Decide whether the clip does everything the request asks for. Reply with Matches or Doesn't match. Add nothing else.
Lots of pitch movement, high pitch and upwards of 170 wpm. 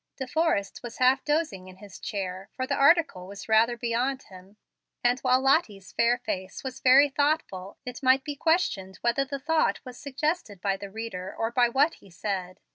Matches